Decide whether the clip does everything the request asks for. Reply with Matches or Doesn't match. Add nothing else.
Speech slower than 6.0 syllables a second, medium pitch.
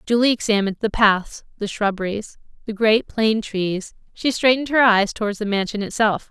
Doesn't match